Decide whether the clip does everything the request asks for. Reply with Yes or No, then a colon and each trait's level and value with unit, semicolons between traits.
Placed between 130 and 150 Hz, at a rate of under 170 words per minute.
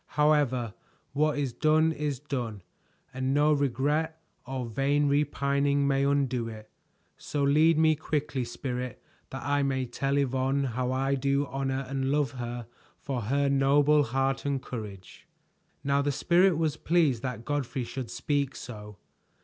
Yes: medium, 140 Hz; average, 150 wpm